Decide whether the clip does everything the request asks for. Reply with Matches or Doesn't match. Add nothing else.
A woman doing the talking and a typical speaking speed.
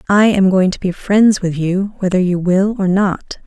Doesn't match